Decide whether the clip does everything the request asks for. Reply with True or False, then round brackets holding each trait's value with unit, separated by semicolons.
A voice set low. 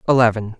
True (115 Hz)